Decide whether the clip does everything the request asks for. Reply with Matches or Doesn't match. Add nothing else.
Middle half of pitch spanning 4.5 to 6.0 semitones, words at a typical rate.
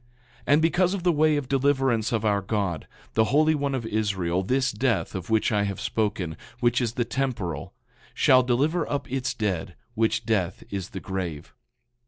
Matches